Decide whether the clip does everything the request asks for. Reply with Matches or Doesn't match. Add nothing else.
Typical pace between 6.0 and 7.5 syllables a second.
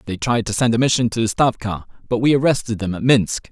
Matches